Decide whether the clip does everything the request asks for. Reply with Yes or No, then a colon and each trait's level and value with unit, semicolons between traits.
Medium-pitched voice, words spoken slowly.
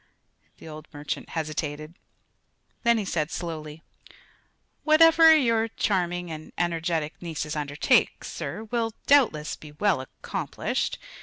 Yes: medium, 165 Hz; slow, 110 wpm